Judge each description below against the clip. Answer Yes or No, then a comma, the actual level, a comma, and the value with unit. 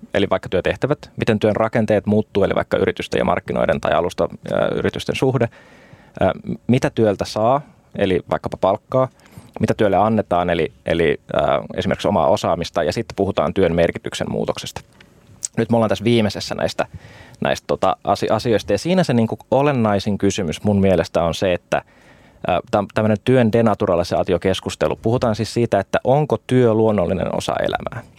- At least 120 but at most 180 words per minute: Yes, average, 150 wpm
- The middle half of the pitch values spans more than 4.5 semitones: No, average, 3.0 semitones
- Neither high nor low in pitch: No, low, 110 Hz